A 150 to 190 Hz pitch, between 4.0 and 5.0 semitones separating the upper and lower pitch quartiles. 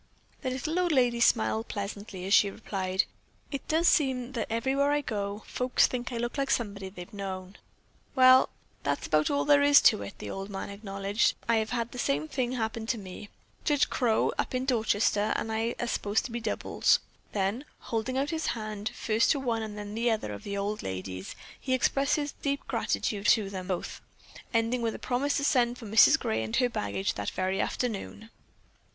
No: high, 225 Hz; average, 4.3 semitones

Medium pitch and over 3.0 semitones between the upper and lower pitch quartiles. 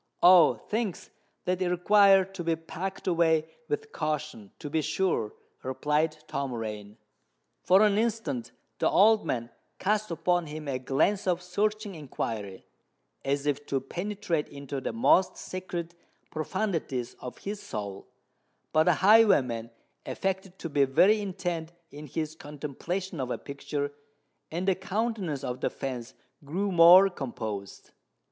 Yes: medium, 165 Hz; wide, 5.6 semitones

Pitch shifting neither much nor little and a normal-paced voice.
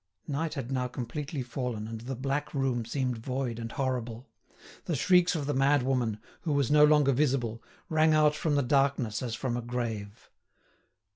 Yes: average, 3.4 semitones; average, 170 wpm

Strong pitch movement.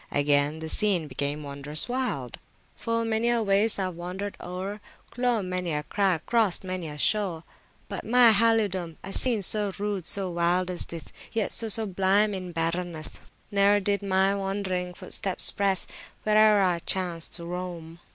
No: average, 3.4 semitones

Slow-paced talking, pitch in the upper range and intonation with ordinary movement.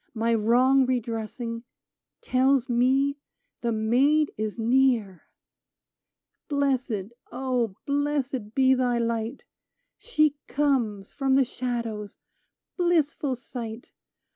Yes: slow, 95 wpm; very high, 250 Hz; average, 3.0 semitones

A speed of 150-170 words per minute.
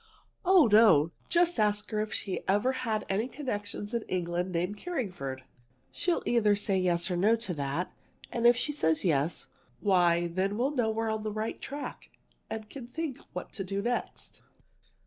No: average, 180 wpm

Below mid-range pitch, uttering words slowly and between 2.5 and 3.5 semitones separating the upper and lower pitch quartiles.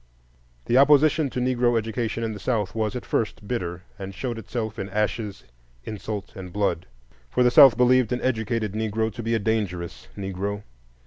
No: low, 110 Hz; average, 175 wpm; average, 3.2 semitones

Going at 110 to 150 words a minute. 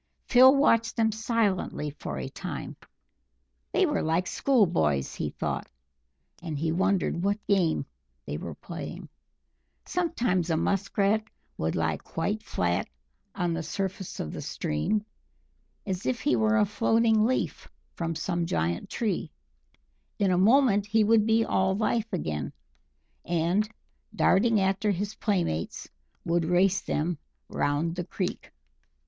Yes: average, 140 wpm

